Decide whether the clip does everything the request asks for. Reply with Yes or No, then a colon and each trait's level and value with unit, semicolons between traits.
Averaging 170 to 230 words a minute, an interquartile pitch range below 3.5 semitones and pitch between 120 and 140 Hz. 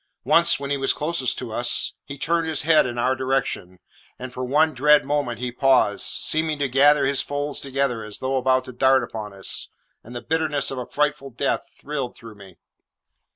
Yes: average, 200 wpm; average, 3.1 semitones; low, 135 Hz